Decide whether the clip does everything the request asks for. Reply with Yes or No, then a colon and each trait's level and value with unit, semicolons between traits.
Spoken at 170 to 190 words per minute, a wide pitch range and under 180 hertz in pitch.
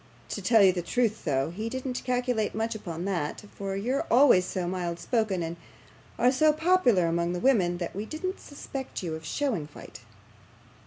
No: average, 180 wpm; wide, 6.4 semitones; high, 205 Hz